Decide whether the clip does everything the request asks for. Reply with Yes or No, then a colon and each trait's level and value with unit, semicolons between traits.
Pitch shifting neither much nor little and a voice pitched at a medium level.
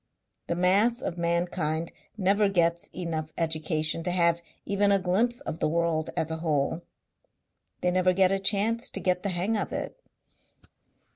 Yes: average, 3.0 semitones; medium, 180 Hz